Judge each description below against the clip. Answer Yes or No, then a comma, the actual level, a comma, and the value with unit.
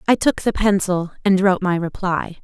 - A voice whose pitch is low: No, high, 190 Hz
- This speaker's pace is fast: No, average, 195 wpm